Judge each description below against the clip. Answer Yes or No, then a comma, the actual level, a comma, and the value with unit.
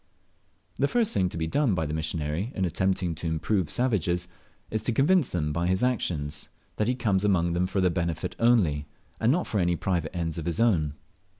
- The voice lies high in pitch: No, very low, 90 Hz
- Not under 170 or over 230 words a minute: Yes, fast, 205 wpm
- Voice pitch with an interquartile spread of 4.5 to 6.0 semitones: Yes, average, 5.2 semitones